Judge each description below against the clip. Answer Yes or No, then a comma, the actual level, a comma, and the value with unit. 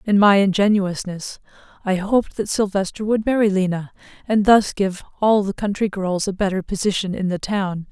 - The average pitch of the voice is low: No, high, 200 Hz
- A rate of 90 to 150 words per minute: No, average, 175 wpm